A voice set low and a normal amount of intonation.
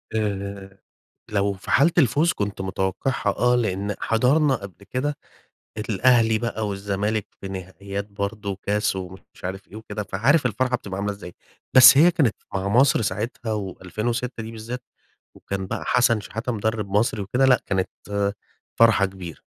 Yes: low, 105 Hz; average, 3.7 semitones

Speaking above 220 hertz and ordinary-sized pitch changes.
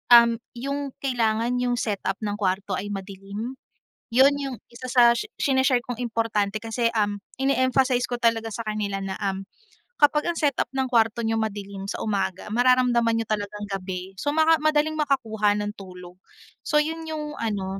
Yes: high, 230 Hz; average, 4.2 semitones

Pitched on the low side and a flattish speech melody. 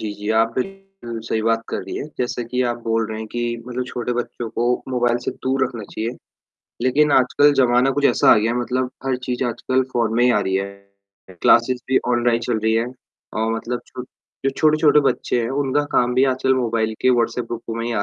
Yes: low, 120 Hz; narrow, 2.1 semitones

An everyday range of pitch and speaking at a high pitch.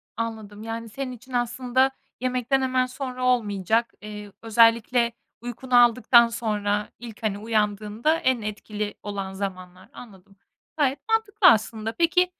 Yes: average, 3.3 semitones; high, 230 Hz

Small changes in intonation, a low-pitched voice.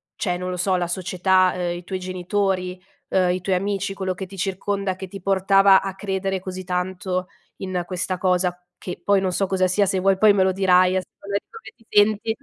No: narrow, 1.2 semitones; high, 190 Hz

